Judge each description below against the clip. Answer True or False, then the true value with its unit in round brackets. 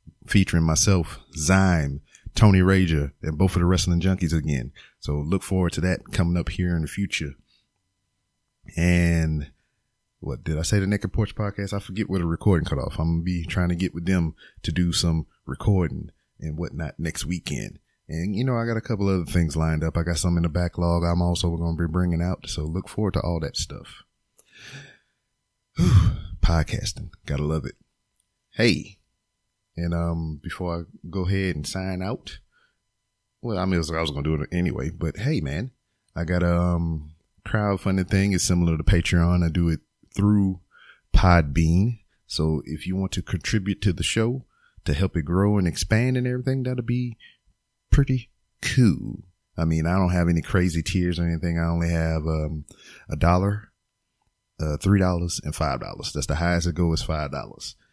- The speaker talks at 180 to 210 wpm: True (185 wpm)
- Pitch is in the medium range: False (90 Hz)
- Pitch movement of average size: True (3.2 semitones)